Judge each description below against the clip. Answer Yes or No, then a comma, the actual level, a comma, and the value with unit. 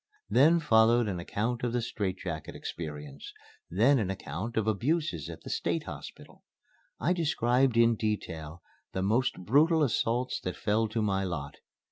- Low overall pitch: Yes, low, 110 Hz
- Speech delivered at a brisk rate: No, average, 155 wpm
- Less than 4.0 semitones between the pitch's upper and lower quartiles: No, average, 5.1 semitones